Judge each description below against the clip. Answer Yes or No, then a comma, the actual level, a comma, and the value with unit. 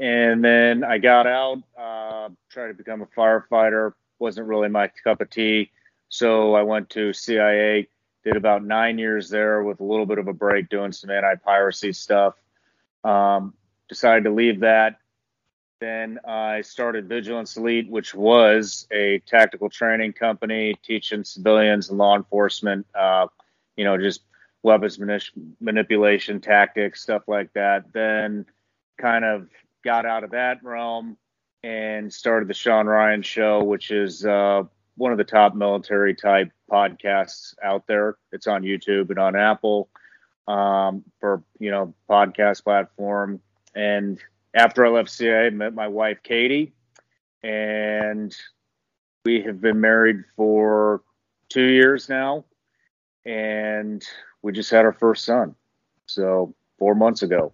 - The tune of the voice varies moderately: No, narrow, 1.8 semitones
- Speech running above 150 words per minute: No, average, 145 wpm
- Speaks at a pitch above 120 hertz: No, low, 105 Hz